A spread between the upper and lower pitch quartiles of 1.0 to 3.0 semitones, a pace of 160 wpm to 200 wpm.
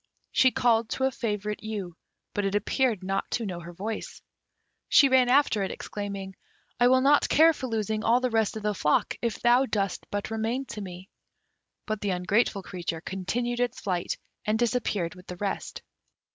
No: average, 3.9 semitones; average, 185 wpm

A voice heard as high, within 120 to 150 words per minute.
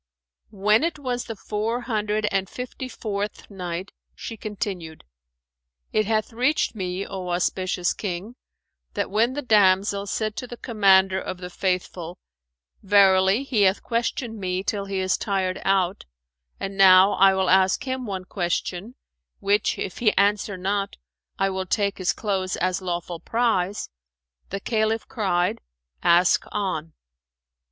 Yes: high, 195 Hz; average, 145 wpm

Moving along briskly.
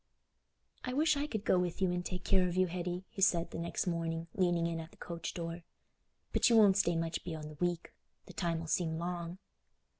Yes: fast, 215 wpm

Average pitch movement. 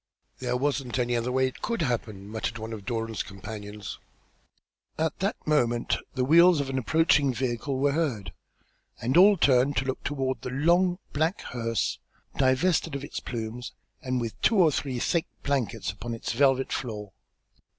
Yes: average, 4.0 semitones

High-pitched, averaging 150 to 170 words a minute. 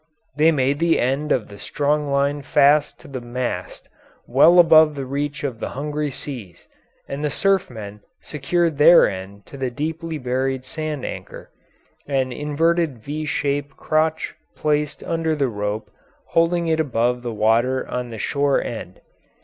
No: medium, 140 Hz; average, 155 wpm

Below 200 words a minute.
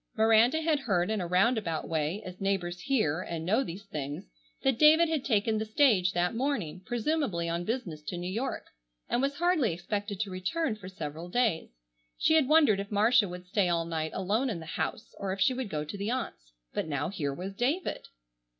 No: fast, 205 wpm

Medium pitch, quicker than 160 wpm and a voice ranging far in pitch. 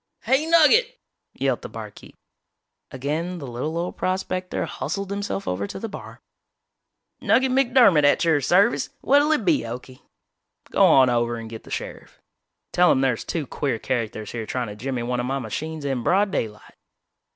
Yes: medium, 150 Hz; average, 170 wpm; wide, 8.4 semitones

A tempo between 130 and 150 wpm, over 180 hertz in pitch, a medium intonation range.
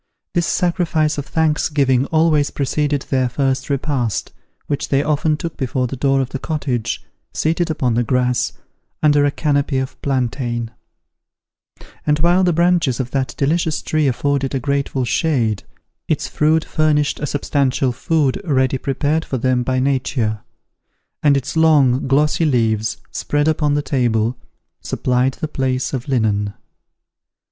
No: average, 145 wpm; medium, 140 Hz; average, 3.0 semitones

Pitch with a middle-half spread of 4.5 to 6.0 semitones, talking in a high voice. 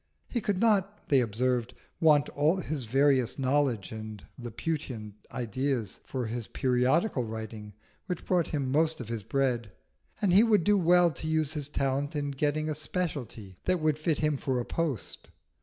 No: average, 4.8 semitones; medium, 140 Hz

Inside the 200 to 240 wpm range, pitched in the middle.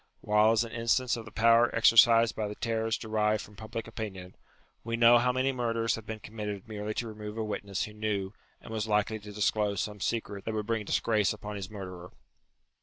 No: fast, 205 wpm; low, 110 Hz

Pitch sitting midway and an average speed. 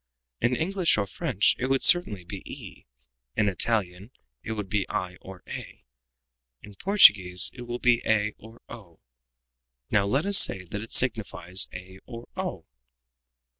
No: low, 105 Hz; average, 155 wpm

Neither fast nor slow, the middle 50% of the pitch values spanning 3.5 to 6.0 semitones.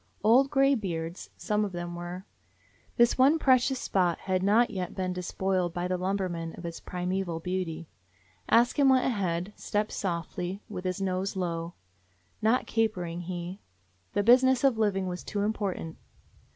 Yes: average, 160 wpm; average, 3.8 semitones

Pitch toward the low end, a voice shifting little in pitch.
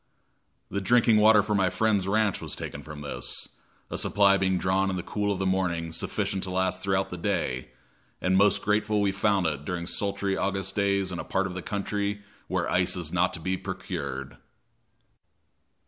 Yes: very low, 95 Hz; narrow, 1.8 semitones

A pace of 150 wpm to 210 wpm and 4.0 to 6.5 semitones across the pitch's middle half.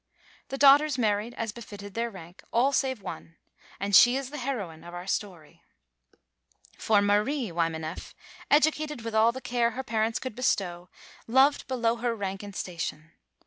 Yes: average, 160 wpm; average, 5.1 semitones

